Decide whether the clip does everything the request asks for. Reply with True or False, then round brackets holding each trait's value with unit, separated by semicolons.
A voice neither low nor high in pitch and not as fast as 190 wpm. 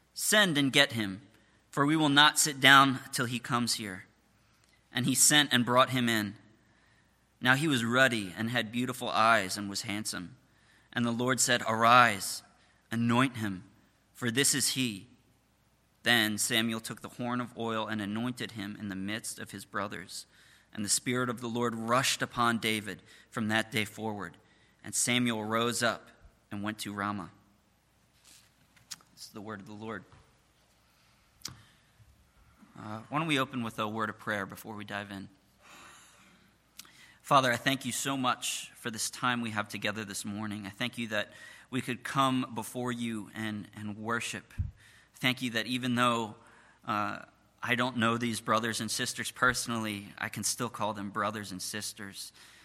False (115 Hz; 170 wpm)